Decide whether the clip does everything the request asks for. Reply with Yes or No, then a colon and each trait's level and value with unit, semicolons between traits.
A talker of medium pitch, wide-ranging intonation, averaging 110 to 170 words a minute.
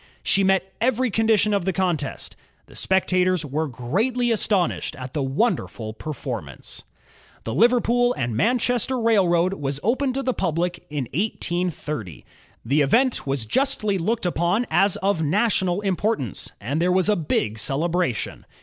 Yes: medium, 180 Hz; wide, 7.2 semitones; average, 145 wpm